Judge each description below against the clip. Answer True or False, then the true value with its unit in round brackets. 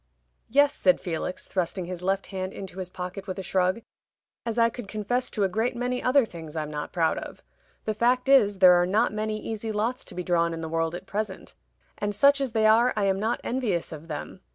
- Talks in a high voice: True (200 Hz)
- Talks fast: True (225 wpm)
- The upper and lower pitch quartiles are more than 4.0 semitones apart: True (4.4 semitones)